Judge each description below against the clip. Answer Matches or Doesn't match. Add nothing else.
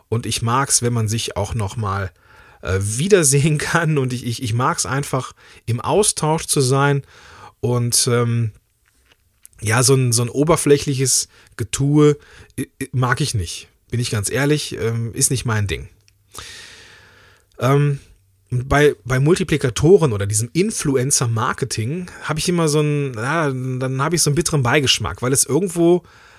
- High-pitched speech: Doesn't match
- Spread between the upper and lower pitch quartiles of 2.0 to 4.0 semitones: Doesn't match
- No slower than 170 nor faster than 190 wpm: Doesn't match